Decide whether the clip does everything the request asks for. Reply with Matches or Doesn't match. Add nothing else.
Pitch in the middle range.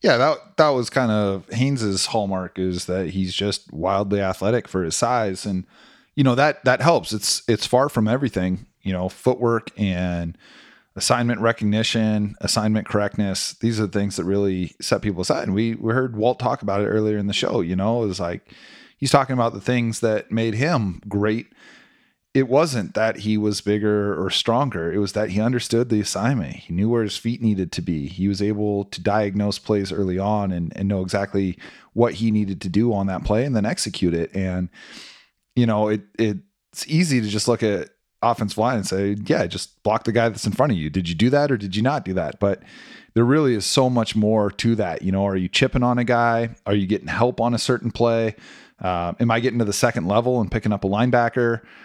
Doesn't match